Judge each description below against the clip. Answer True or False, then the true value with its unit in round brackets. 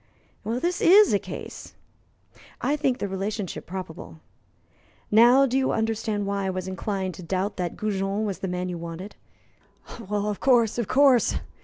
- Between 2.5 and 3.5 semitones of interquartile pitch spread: False (4.2 semitones)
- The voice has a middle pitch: False (205 Hz)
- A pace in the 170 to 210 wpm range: False (155 wpm)